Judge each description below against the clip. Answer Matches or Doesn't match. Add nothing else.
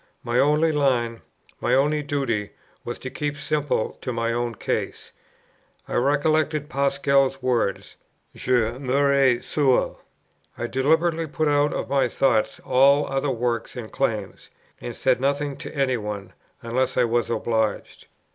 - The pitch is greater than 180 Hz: Doesn't match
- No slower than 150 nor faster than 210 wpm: Doesn't match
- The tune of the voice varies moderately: Matches